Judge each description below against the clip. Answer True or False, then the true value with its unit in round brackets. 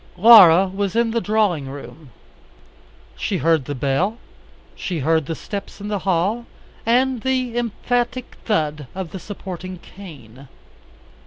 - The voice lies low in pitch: False (190 Hz)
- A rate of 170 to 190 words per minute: False (135 wpm)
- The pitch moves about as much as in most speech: False (5.9 semitones)